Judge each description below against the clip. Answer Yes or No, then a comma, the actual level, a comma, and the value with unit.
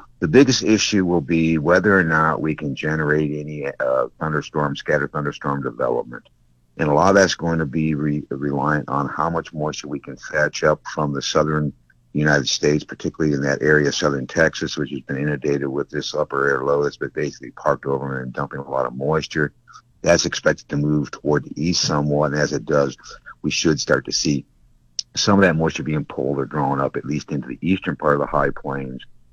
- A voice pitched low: Yes, very low, 75 Hz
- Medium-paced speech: No, fast, 210 wpm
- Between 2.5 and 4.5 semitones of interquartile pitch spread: No, narrow, 1.9 semitones